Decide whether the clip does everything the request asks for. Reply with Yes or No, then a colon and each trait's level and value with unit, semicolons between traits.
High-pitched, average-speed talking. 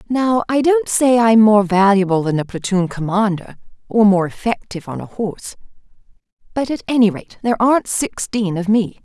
Yes: high, 210 Hz; average, 175 wpm